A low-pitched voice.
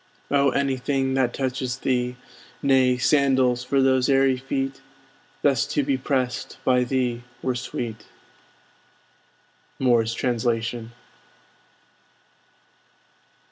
Yes: low, 130 Hz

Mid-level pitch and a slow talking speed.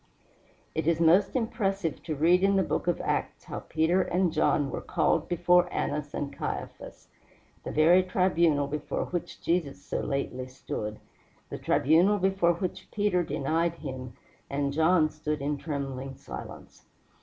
No: medium, 160 Hz; average, 150 wpm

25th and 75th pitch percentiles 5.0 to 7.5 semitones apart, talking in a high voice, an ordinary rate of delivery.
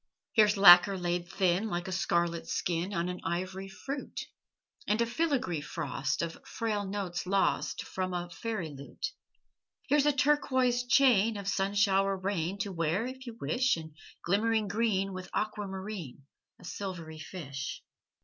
No: average, 3.9 semitones; high, 195 Hz; average, 150 wpm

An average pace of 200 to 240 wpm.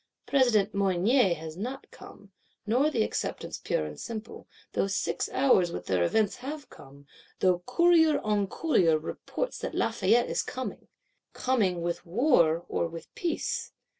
No: average, 145 wpm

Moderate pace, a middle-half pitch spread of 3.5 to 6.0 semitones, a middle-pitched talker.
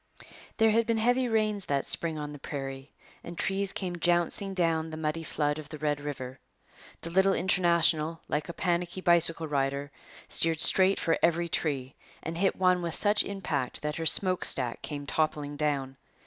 Yes: average, 175 wpm; average, 3.9 semitones; medium, 165 Hz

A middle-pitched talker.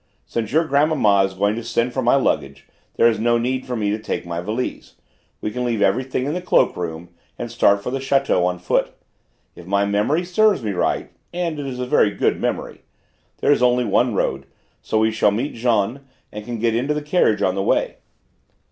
No: low, 115 Hz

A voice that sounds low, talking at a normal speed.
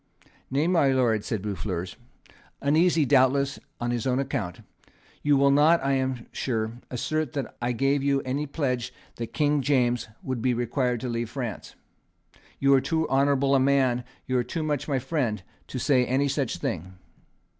Yes: low, 130 Hz; average, 170 wpm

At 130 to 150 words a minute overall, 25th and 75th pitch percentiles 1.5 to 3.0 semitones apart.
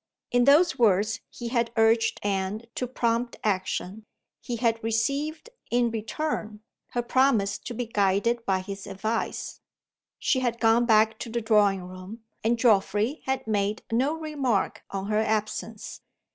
Yes: average, 145 wpm; narrow, 2.6 semitones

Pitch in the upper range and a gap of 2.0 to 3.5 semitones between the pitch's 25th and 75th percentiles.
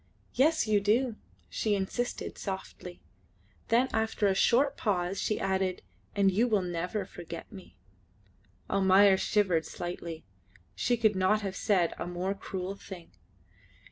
Yes: high, 195 Hz; average, 2.9 semitones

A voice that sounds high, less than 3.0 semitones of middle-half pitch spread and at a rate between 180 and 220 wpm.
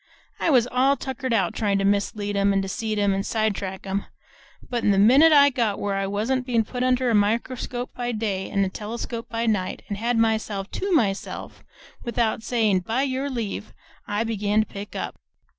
No: high, 220 Hz; average, 3.5 semitones; average, 190 wpm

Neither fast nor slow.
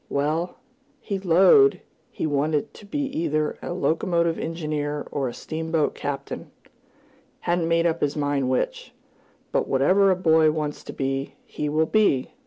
Yes: average, 150 wpm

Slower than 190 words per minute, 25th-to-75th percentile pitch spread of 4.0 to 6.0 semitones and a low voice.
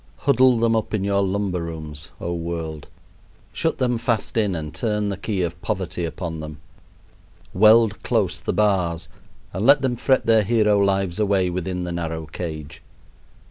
Yes: average, 165 wpm; average, 4.4 semitones; very low, 95 Hz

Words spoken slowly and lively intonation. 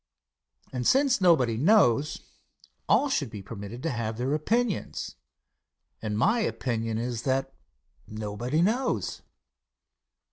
Yes: slow, 110 wpm; wide, 8.3 semitones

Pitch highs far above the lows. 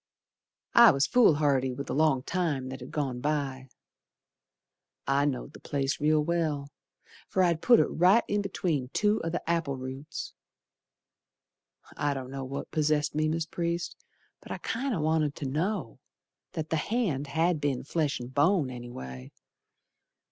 No: average, 3.9 semitones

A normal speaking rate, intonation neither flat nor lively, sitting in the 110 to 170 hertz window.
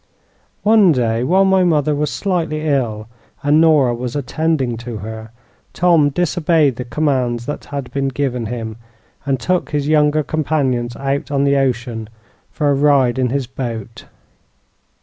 Yes: average, 150 wpm; average, 3.9 semitones; medium, 140 Hz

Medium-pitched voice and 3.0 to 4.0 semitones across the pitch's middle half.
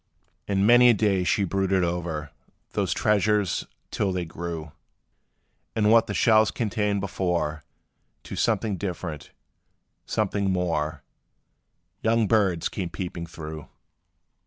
No: very low, 95 Hz; average, 3.7 semitones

